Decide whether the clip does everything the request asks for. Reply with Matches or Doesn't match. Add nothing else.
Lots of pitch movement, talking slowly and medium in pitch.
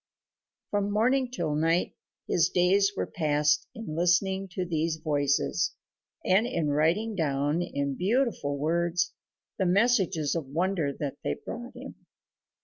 Doesn't match